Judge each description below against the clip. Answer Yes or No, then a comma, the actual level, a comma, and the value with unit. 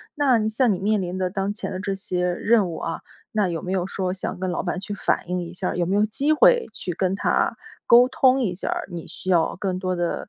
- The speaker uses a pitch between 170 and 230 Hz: Yes, high, 190 Hz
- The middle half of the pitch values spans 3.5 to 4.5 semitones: No, average, 3.1 semitones